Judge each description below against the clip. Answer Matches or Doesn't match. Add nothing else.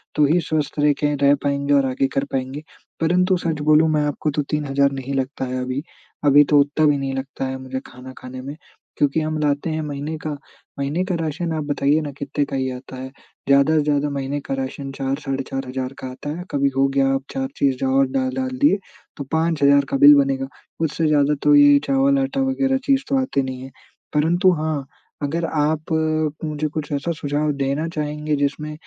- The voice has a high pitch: Doesn't match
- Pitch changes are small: Matches